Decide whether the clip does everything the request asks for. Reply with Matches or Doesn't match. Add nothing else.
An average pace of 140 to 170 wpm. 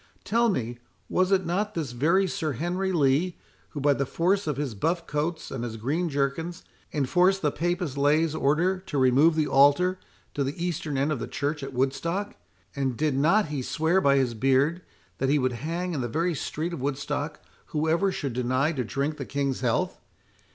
Doesn't match